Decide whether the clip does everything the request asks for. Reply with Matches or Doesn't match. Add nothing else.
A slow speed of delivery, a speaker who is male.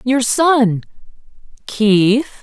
Doesn't match